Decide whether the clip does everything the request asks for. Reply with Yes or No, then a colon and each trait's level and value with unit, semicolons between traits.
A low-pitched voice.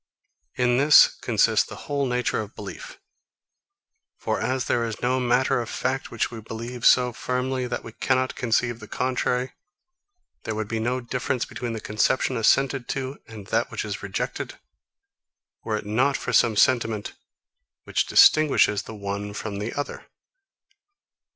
Yes: low, 120 Hz